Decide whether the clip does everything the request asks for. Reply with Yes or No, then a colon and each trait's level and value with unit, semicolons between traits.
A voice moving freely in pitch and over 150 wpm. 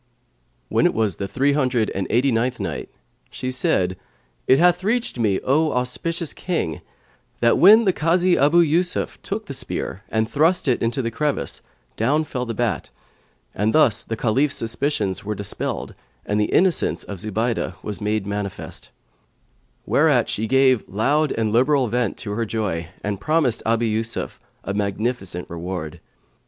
Yes: wide, 5.9 semitones; average, 160 wpm